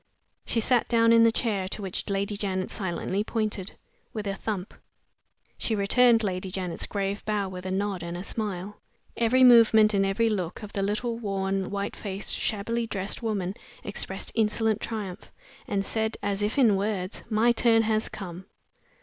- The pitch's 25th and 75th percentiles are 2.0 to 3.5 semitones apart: Yes, narrow, 2.5 semitones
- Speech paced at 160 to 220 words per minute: Yes, average, 170 wpm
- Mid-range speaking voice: No, high, 205 Hz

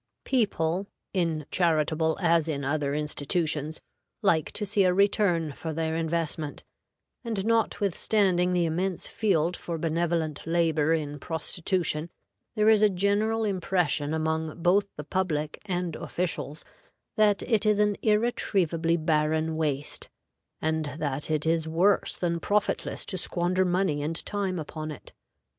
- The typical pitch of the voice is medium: Yes, medium, 165 Hz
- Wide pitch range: No, average, 3.6 semitones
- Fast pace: No, slow, 135 wpm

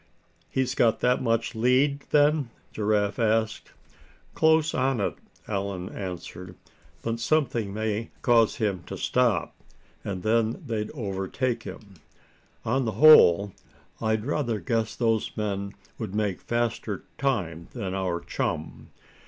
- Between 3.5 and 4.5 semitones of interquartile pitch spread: Yes, average, 3.9 semitones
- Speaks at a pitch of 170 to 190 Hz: No, low, 110 Hz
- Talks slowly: Yes, slow, 125 wpm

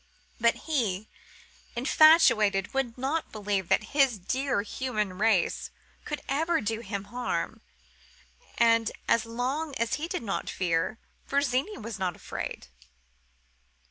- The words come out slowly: Yes, slow, 120 wpm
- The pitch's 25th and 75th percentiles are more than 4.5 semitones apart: Yes, average, 4.9 semitones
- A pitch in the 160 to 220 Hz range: No, high, 230 Hz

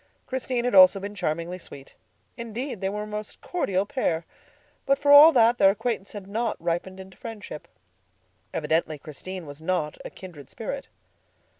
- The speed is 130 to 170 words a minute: Yes, average, 160 wpm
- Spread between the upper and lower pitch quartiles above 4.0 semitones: Yes, average, 5.1 semitones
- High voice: Yes, high, 195 Hz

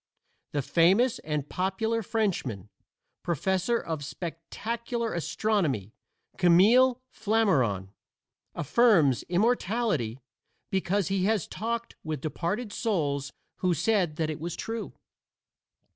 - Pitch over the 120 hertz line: Yes, medium, 185 Hz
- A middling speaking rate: No, slow, 100 wpm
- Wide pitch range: Yes, wide, 6.4 semitones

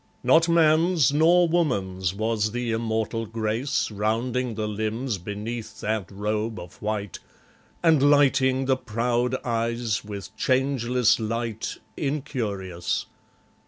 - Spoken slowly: Yes, slow, 110 wpm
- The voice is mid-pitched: No, low, 115 Hz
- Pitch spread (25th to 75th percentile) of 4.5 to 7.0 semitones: No, average, 3.7 semitones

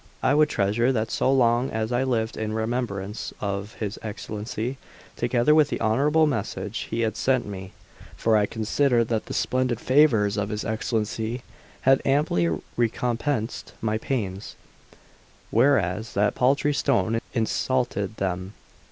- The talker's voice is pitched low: Yes, low, 115 Hz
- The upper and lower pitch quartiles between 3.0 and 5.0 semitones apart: Yes, average, 3.5 semitones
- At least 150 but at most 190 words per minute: No, average, 140 wpm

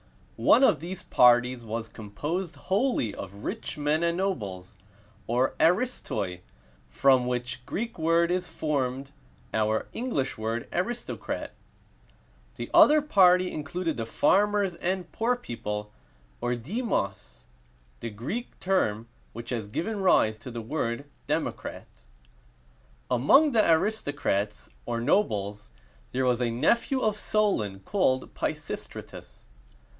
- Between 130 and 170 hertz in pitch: Yes, medium, 140 Hz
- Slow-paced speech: Yes, slow, 120 wpm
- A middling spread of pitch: No, wide, 8.8 semitones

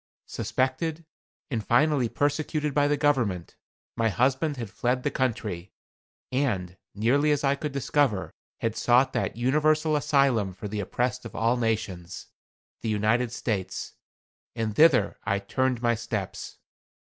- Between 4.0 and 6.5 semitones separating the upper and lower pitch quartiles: Yes, average, 4.8 semitones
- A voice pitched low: Yes, low, 125 Hz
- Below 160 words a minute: Yes, slow, 135 wpm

